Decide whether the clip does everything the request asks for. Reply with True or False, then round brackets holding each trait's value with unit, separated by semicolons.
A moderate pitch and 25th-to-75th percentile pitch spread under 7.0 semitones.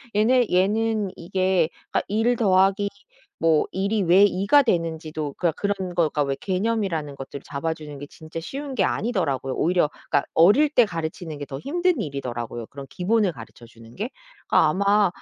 True (180 Hz; 5.4 semitones)